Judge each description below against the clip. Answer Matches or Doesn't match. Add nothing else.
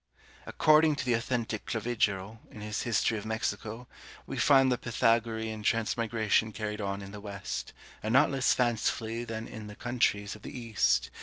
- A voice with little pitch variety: Matches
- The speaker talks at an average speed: Matches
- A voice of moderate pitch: Doesn't match